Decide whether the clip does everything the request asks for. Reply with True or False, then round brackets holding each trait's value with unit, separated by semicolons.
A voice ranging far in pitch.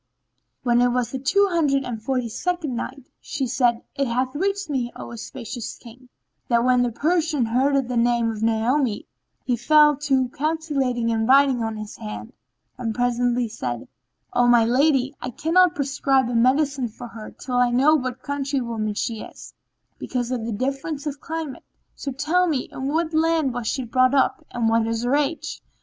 False (3.3 semitones)